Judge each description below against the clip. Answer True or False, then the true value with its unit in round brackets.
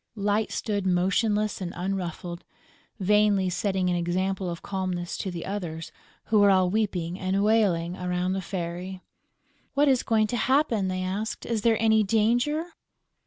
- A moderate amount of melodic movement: True (3.1 semitones)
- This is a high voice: True (195 Hz)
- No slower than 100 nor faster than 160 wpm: True (155 wpm)